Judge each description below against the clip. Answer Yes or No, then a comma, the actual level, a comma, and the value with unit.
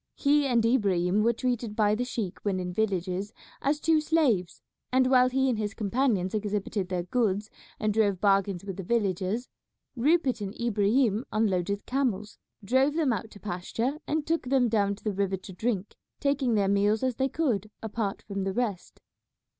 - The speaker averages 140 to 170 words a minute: No, average, 185 wpm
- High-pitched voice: Yes, high, 215 Hz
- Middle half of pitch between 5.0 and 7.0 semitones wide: No, average, 4.3 semitones